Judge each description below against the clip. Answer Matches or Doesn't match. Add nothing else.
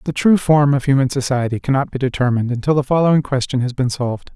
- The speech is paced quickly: Matches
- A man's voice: Matches